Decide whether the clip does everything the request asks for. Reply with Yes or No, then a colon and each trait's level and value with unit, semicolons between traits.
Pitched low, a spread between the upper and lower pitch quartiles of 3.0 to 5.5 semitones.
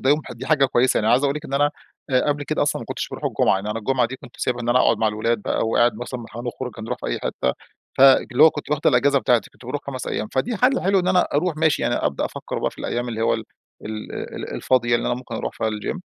Yes: low, 125 Hz; average, 3.7 semitones